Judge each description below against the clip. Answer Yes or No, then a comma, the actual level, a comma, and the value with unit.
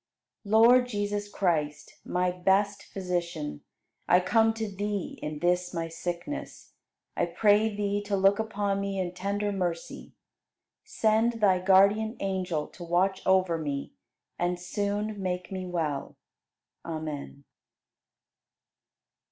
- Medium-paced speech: No, slow, 120 wpm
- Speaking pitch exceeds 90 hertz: Yes, high, 190 Hz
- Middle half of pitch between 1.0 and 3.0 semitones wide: Yes, average, 2.7 semitones